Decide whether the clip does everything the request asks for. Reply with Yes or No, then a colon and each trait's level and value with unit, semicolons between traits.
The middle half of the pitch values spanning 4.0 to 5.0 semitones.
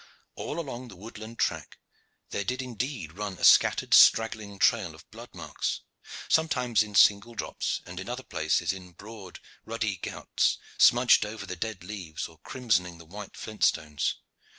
Yes: average, 4.4 semitones